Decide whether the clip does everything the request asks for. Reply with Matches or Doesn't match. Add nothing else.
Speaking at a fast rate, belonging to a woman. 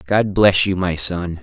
Doesn't match